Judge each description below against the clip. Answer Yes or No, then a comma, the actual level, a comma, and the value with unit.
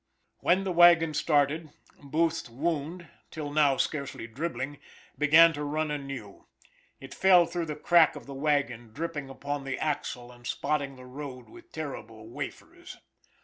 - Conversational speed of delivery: Yes, average, 145 wpm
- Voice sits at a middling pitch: Yes, medium, 145 Hz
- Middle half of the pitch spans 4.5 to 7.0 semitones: No, average, 3.3 semitones